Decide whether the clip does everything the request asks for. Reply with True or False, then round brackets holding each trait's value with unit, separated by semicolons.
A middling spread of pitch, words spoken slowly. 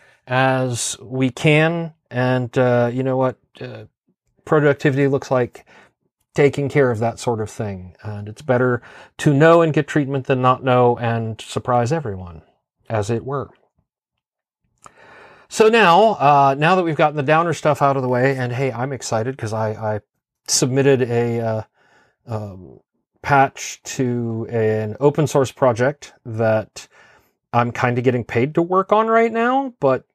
False (4.0 semitones; 155 wpm)